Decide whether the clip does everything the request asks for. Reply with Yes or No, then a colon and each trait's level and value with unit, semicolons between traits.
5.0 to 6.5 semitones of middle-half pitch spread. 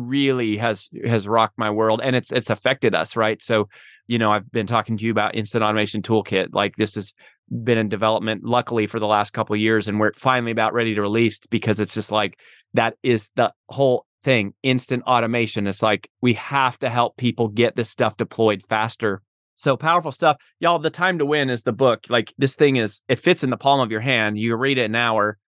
No: average, 2.8 semitones